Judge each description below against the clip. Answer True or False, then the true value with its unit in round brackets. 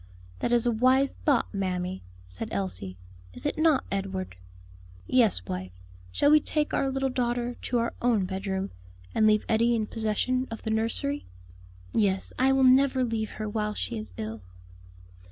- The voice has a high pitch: True (225 Hz)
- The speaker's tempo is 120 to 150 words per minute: False (165 wpm)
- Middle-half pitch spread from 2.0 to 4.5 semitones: False (5.1 semitones)